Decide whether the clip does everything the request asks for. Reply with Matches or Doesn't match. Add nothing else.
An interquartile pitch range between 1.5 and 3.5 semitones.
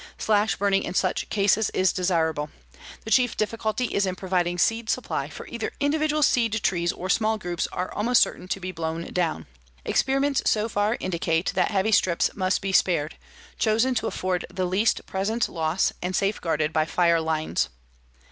Doesn't match